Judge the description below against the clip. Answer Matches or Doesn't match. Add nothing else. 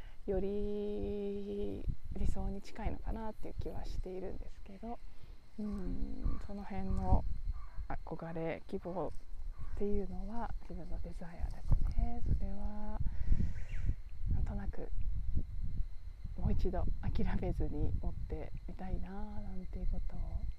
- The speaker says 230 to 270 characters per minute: Matches